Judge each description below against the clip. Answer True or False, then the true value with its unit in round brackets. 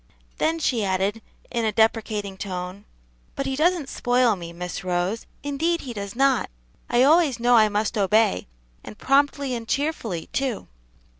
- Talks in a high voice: True (230 Hz)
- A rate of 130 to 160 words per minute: True (155 wpm)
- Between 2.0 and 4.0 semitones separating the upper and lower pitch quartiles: False (5.4 semitones)